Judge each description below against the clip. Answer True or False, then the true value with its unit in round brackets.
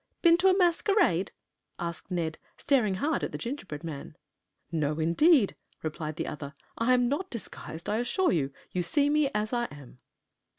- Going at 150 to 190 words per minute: True (170 wpm)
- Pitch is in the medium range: False (210 Hz)